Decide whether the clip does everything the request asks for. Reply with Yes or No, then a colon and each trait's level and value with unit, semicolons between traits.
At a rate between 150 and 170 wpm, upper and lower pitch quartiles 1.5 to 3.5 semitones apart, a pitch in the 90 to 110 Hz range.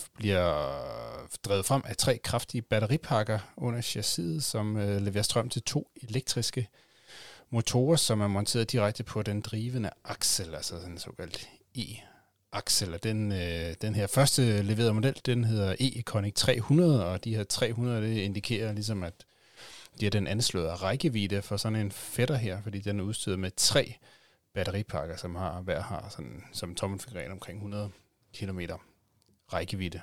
Yes: average, 155 wpm; average, 3.2 semitones; low, 105 Hz